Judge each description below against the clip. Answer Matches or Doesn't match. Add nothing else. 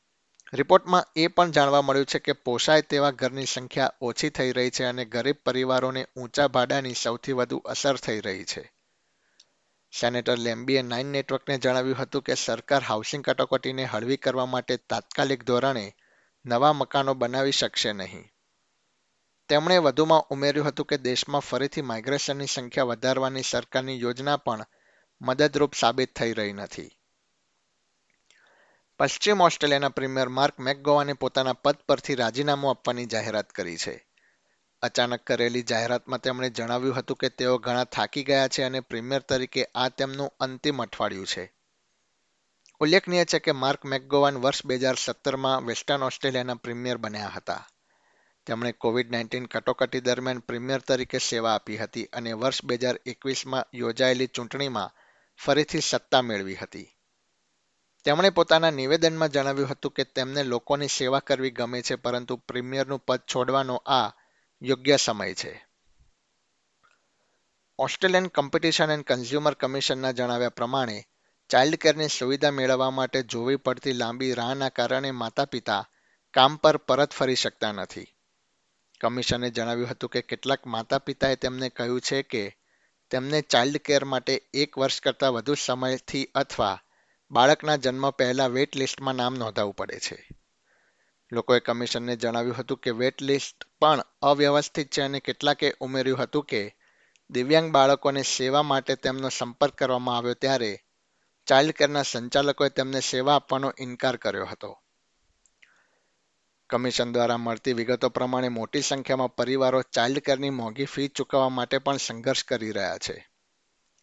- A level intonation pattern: Matches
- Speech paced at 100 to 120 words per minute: Doesn't match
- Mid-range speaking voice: Doesn't match